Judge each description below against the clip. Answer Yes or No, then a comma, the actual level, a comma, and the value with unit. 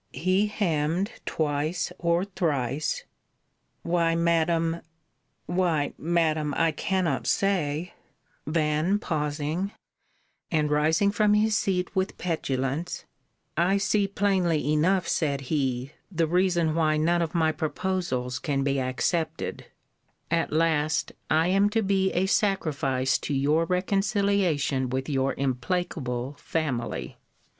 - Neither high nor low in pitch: Yes, medium, 165 Hz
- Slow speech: Yes, slow, 115 wpm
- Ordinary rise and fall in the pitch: Yes, average, 3.9 semitones